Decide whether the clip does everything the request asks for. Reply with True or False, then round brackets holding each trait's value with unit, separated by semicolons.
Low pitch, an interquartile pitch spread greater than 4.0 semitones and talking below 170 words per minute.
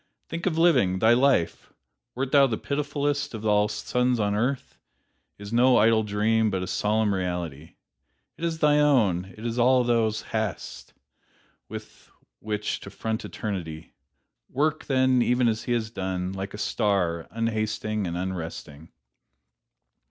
True (110 Hz; 4.6 semitones; 150 wpm)